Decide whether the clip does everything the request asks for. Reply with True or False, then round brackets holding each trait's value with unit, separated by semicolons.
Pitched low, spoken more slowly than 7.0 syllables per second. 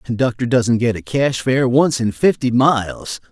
True (125 Hz; 4.5 syllables/s)